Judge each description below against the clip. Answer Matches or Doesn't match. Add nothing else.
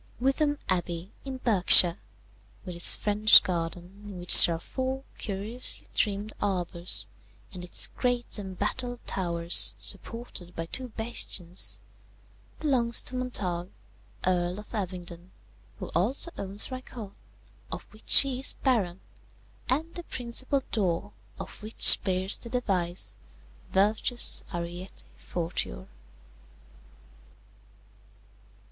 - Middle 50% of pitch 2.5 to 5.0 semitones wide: Doesn't match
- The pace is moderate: Doesn't match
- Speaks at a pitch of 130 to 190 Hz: Doesn't match